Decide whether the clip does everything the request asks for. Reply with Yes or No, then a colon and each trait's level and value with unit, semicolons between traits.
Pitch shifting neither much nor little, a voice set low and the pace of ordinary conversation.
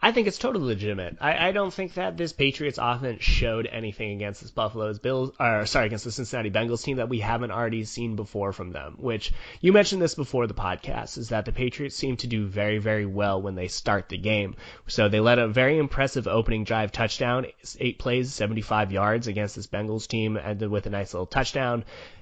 No: average, 3.5 semitones; low, 115 Hz; fast, 215 wpm